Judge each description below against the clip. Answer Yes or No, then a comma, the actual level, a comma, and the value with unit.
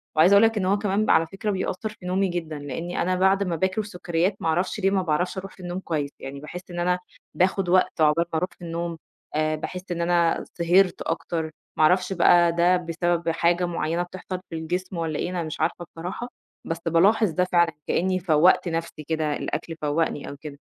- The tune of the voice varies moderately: No, narrow, 2.2 semitones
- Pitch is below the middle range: No, medium, 175 Hz